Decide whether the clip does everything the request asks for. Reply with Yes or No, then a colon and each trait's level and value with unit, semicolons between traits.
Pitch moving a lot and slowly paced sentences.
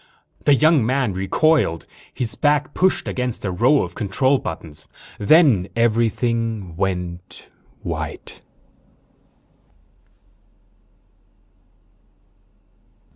Yes: wide, 6.7 semitones; slow, 80 wpm